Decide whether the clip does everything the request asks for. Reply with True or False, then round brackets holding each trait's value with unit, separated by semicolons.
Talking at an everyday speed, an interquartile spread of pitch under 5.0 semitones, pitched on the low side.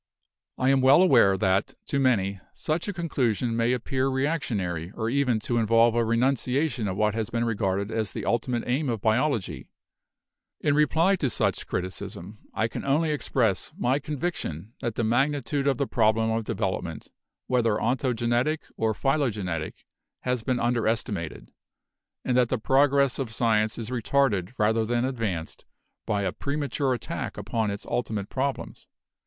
True (160 wpm; 3.9 semitones; 120 Hz)